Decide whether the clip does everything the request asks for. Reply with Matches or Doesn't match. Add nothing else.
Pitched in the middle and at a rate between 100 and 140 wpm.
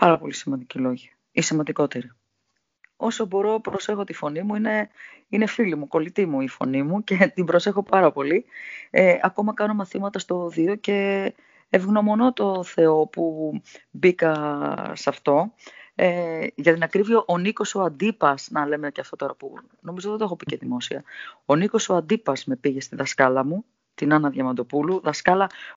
Doesn't match